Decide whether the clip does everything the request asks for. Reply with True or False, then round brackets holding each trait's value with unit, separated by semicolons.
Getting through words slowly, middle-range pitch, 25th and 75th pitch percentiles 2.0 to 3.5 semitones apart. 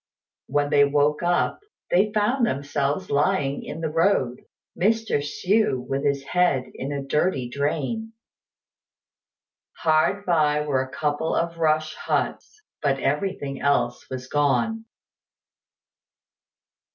False (115 wpm; 150 Hz; 4.3 semitones)